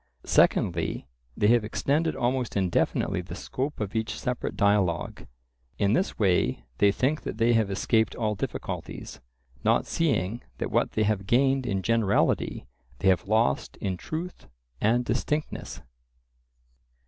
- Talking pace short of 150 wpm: Yes, slow, 135 wpm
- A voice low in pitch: Yes, low, 110 Hz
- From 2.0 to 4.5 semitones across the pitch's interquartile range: Yes, average, 4.2 semitones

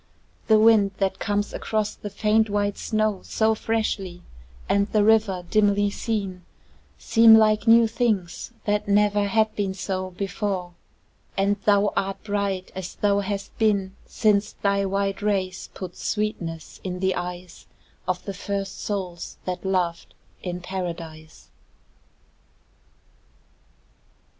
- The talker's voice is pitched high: Yes, high, 200 Hz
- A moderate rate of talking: No, slow, 125 wpm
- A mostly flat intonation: Yes, narrow, 2.2 semitones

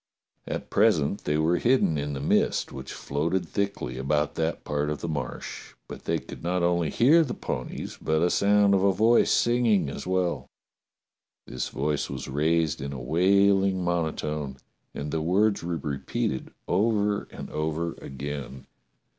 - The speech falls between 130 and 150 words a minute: No, average, 165 wpm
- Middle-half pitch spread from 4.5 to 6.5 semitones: Yes, average, 5.1 semitones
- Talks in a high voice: No, very low, 80 Hz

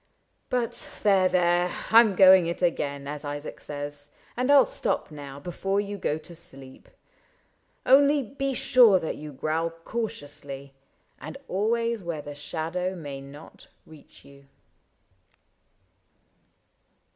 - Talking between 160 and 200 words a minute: No, slow, 135 wpm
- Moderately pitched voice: Yes, medium, 170 Hz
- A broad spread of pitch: Yes, wide, 6.0 semitones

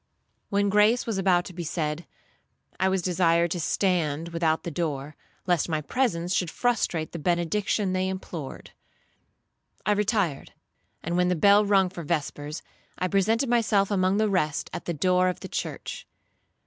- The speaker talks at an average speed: Yes, average, 160 wpm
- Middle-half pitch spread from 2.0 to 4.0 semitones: Yes, average, 3.1 semitones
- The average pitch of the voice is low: No, medium, 180 Hz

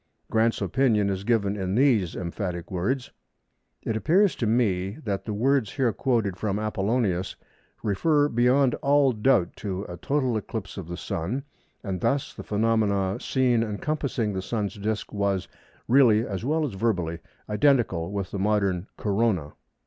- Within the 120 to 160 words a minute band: Yes, average, 150 wpm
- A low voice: Yes, low, 105 Hz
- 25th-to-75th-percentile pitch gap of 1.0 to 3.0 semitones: No, average, 4.3 semitones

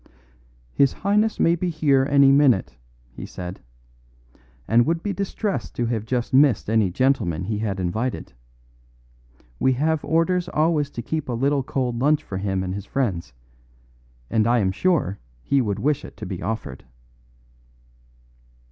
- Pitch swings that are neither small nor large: No, wide, 6.7 semitones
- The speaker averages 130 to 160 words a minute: Yes, average, 155 wpm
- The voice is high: No, low, 130 Hz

